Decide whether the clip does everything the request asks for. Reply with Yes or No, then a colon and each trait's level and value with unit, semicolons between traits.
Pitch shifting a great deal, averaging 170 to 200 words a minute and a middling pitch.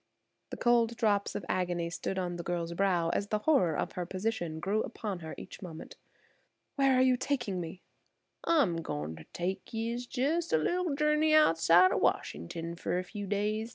No: wide, 5.7 semitones; average, 185 wpm; high, 195 Hz